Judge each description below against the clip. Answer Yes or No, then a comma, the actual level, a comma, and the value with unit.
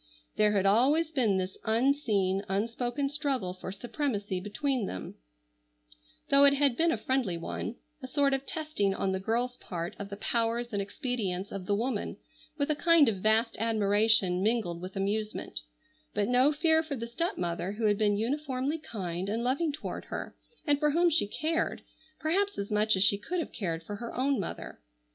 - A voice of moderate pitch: No, high, 225 Hz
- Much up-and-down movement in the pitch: Yes, wide, 5.9 semitones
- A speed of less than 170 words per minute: No, average, 180 wpm